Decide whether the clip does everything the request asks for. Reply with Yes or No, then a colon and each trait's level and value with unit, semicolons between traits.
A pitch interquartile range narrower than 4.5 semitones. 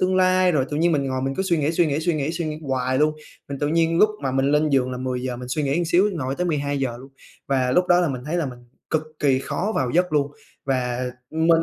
Yes: average, 4.1 semitones